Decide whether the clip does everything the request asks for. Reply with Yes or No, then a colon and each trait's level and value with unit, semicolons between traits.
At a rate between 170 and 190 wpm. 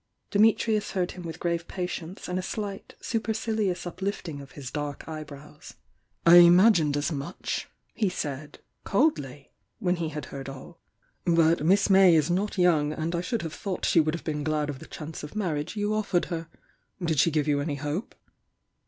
Yes: average, 185 wpm